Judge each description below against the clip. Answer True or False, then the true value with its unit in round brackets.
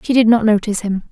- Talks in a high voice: True (220 Hz)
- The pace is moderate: False (270 wpm)